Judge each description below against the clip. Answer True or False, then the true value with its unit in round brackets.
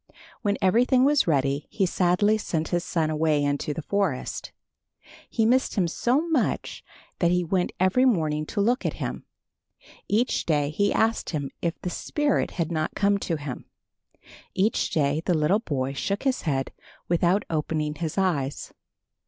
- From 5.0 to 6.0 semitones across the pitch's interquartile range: True (5.3 semitones)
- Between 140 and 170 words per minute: True (160 wpm)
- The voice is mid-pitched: True (175 Hz)